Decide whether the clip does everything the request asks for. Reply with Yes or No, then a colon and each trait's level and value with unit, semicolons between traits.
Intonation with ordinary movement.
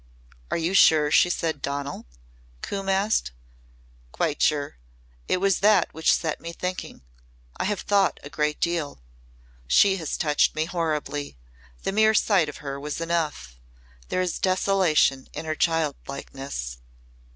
Yes: average, 4.2 semitones